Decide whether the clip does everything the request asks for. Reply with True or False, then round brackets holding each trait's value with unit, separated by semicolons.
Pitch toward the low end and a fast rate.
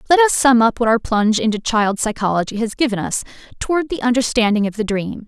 False (230 Hz; 215 wpm)